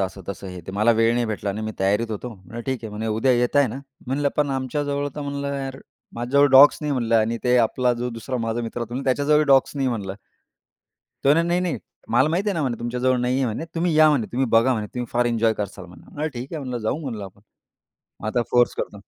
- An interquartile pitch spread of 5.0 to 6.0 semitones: No, average, 4.0 semitones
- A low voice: Yes, low, 125 Hz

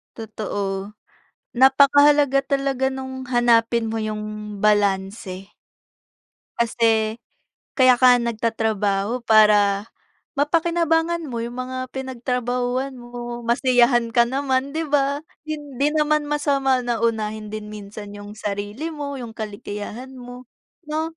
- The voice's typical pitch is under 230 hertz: No, high, 245 Hz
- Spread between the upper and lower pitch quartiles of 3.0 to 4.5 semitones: Yes, average, 4.1 semitones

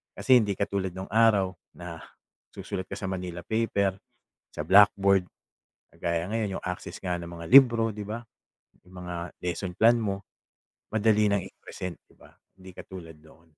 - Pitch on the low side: Yes, very low, 95 Hz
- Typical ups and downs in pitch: Yes, average, 3.2 semitones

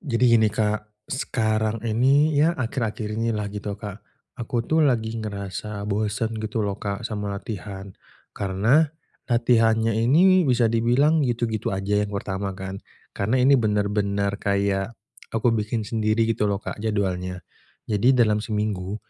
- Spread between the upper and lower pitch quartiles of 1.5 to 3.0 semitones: Yes, narrow, 2.5 semitones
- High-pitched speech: No, low, 110 Hz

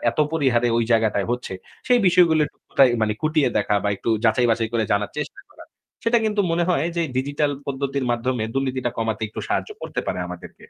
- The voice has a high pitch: No, low, 130 Hz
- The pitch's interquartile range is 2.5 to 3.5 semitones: No, average, 5.3 semitones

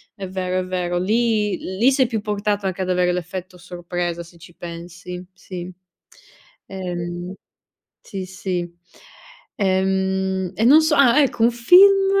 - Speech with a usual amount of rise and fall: Yes, average, 3.0 semitones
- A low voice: No, medium, 185 Hz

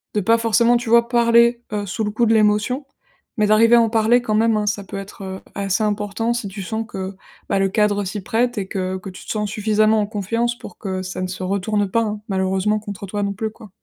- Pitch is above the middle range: Yes, high, 210 Hz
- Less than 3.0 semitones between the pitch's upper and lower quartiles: Yes, narrow, 2.4 semitones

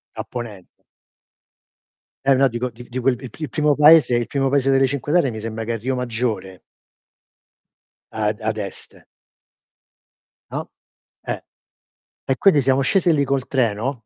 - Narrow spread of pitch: No, average, 3.4 semitones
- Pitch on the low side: Yes, low, 125 Hz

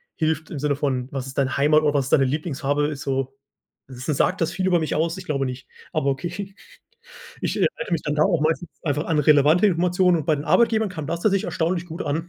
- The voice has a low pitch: No, medium, 155 Hz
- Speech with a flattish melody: No, average, 3.7 semitones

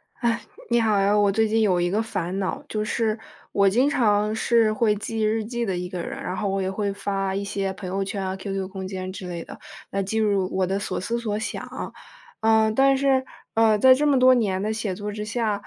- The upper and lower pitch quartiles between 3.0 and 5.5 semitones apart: No, narrow, 2.5 semitones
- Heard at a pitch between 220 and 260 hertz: No, high, 210 Hz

